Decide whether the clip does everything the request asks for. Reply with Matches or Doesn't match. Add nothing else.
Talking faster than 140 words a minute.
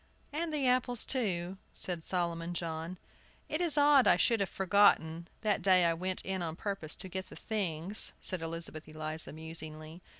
Matches